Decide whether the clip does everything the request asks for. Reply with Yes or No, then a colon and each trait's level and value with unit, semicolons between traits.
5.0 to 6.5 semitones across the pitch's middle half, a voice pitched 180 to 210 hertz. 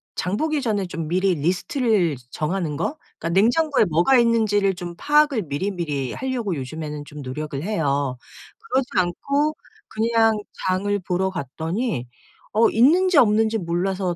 Yes: wide, 6.1 semitones; high, 190 Hz